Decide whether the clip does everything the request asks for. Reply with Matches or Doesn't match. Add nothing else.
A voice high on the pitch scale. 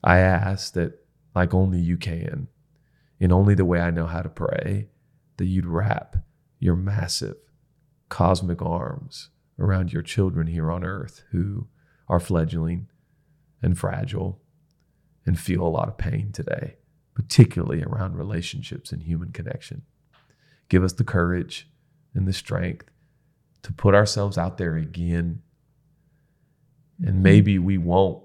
Doesn't match